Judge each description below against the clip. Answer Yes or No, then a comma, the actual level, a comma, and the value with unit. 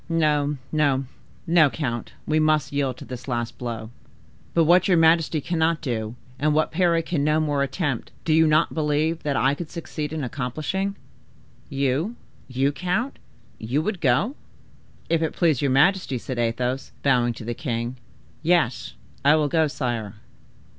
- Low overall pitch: No, medium, 150 Hz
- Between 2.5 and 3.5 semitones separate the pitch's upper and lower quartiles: No, average, 4.2 semitones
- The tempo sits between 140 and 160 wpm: Yes, average, 155 wpm